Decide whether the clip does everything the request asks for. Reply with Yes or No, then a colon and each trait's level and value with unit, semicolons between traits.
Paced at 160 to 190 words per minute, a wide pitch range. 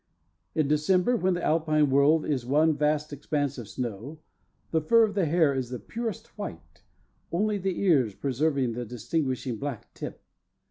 No: average, 165 wpm; average, 4.5 semitones